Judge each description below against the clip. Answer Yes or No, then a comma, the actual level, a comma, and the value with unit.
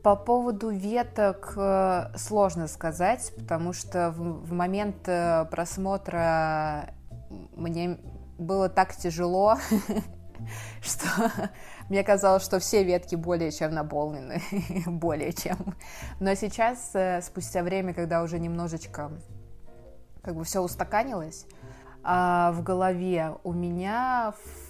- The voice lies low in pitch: No, medium, 175 Hz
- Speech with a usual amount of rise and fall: Yes, average, 3.0 semitones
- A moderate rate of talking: No, slow, 100 wpm